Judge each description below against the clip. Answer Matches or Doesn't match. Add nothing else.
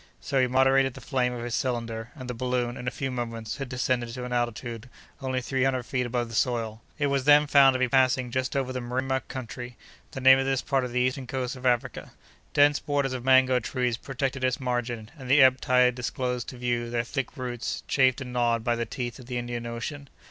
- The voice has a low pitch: Matches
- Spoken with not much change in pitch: Matches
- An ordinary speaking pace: Doesn't match